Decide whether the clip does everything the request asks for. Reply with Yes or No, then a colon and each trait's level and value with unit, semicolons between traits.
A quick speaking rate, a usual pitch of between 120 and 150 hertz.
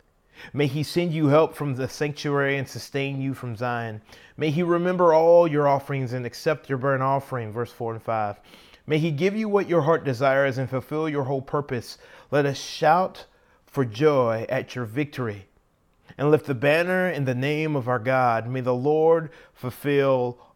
No: average, 185 wpm; medium, 140 Hz